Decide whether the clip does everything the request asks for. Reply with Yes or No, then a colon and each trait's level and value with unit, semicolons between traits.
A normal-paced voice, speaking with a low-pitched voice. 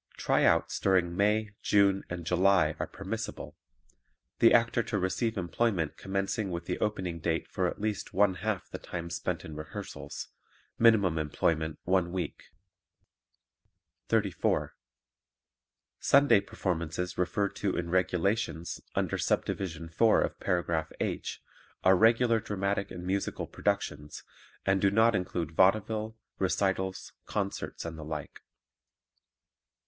No: slow, 125 wpm; very low, 95 Hz